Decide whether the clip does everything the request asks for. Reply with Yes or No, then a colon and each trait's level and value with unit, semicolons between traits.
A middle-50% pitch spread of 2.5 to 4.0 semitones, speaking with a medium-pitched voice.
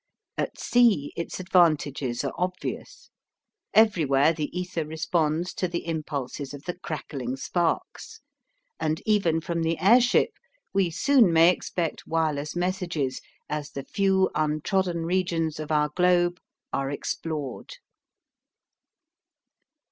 Yes: average, 3.3 semitones; medium, 165 Hz